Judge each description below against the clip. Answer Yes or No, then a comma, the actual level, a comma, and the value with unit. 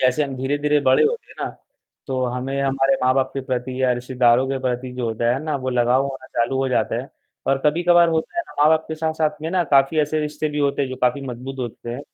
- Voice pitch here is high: No, low, 135 Hz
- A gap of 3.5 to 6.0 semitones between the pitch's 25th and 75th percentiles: No, average, 2.8 semitones